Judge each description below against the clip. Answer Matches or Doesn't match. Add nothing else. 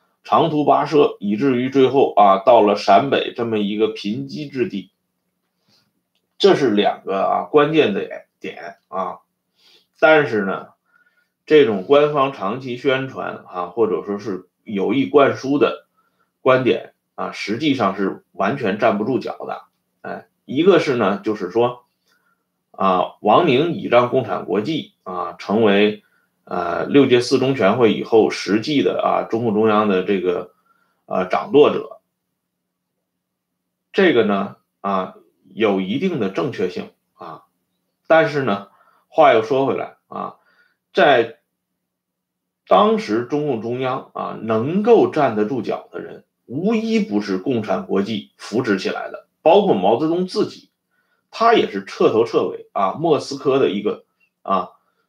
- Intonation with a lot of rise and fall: Matches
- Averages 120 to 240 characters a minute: Matches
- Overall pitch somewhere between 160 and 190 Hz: Doesn't match